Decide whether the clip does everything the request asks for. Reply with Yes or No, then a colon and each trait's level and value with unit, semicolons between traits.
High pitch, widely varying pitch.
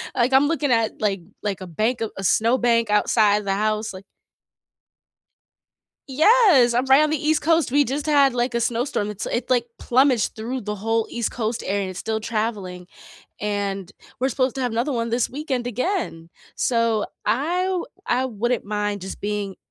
No: high, 235 Hz; average, 3.9 semitones